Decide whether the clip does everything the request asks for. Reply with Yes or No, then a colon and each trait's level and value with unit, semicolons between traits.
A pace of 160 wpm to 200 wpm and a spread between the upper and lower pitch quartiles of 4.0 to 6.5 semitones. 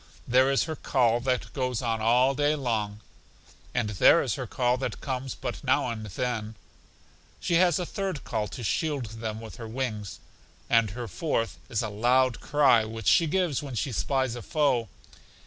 No: average, 180 wpm; average, 3.5 semitones